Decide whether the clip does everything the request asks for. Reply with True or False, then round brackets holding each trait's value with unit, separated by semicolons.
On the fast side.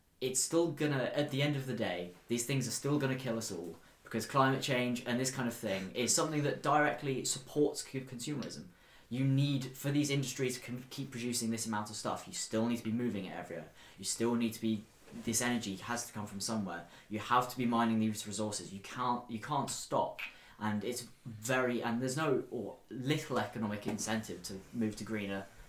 True (210 wpm)